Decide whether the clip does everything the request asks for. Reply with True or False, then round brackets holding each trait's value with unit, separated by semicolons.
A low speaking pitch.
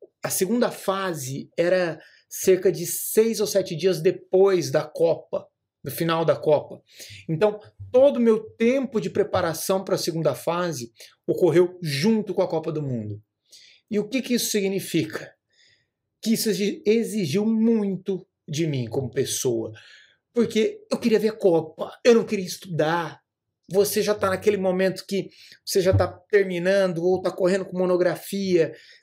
False (185 Hz)